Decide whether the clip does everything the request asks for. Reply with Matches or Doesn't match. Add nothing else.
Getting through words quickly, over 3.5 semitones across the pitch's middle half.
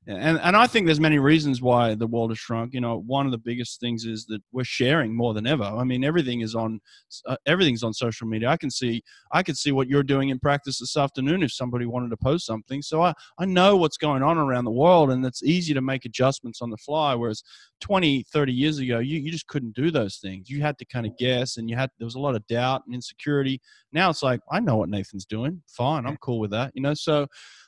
Matches